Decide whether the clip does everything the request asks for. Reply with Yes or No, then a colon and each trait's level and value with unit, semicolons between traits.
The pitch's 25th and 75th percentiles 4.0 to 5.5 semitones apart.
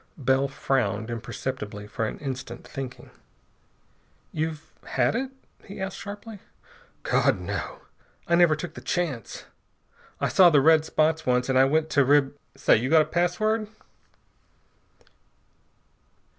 Yes: average, 5.0 semitones